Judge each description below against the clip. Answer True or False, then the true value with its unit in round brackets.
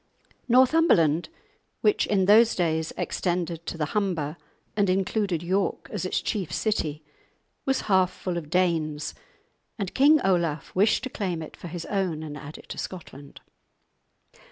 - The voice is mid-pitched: True (180 Hz)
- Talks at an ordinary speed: True (150 wpm)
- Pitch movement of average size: True (4.2 semitones)